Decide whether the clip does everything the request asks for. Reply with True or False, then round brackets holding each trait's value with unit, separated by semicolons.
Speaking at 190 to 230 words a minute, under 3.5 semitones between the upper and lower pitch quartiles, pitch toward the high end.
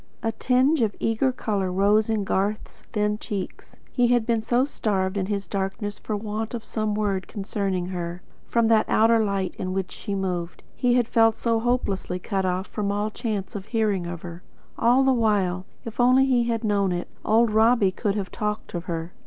True (200 wpm; 3.1 semitones; 210 Hz)